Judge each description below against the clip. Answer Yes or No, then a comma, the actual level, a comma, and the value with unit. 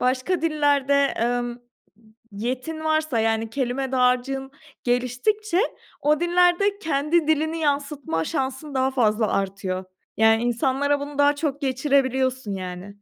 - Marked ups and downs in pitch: No, average, 3.7 semitones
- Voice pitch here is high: Yes, very high, 265 Hz